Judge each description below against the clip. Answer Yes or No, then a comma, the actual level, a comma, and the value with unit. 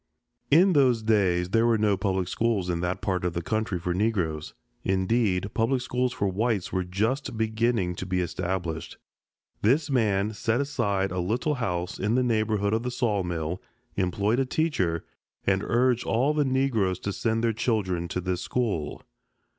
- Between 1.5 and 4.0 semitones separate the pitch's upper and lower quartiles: No, average, 4.5 semitones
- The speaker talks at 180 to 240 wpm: No, average, 170 wpm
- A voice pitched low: Yes, low, 105 Hz